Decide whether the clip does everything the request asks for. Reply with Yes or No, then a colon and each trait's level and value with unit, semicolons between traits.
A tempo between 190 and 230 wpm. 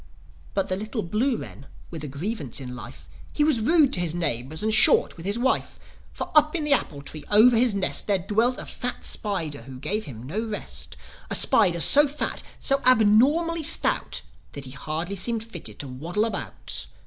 Yes: average, 195 wpm